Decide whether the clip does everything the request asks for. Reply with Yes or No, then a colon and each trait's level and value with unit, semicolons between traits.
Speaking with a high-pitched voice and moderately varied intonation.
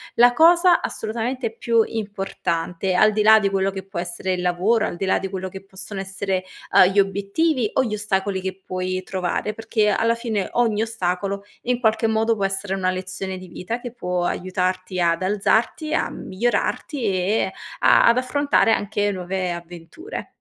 Yes: high, 195 Hz; average, 3.4 semitones